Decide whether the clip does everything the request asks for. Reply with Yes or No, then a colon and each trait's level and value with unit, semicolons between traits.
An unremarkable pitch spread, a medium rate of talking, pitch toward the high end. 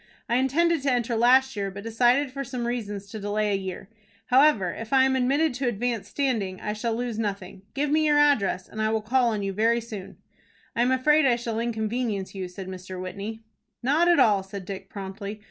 No: average, 4.5 semitones; fast, 215 wpm; high, 230 Hz